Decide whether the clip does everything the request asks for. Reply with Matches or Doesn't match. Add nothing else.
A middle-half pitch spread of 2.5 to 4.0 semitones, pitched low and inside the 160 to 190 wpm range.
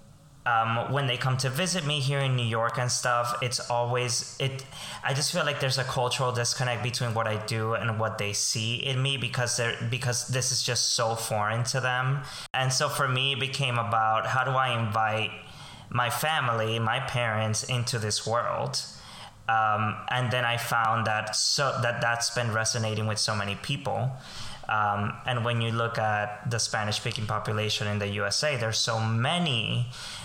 Matches